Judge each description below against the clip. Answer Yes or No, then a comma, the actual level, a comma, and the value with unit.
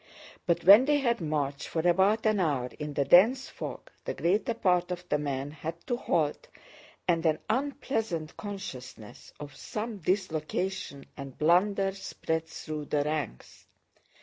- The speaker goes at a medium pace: Yes, average, 150 wpm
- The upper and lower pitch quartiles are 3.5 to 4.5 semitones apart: No, average, 5.3 semitones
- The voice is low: No, medium, 170 Hz